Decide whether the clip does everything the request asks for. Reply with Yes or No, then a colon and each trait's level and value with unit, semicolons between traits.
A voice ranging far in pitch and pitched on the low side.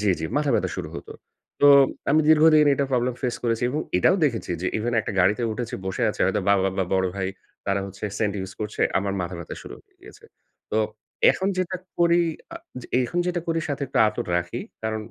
Yes: wide, 7.4 semitones; low, 115 Hz